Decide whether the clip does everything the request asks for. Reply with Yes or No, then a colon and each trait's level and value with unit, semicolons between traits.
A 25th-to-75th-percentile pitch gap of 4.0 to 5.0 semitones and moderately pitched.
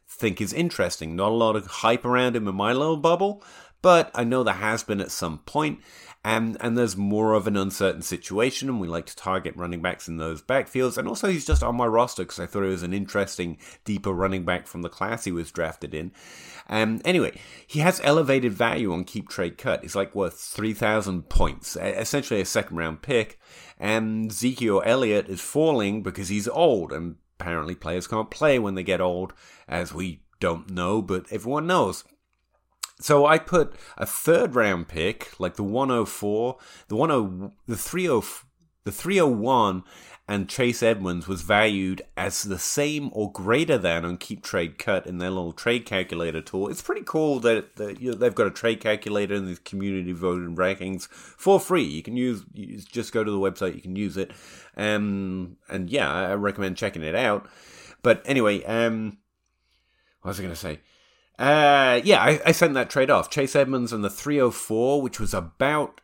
No: average, 4.7 semitones; low, 105 Hz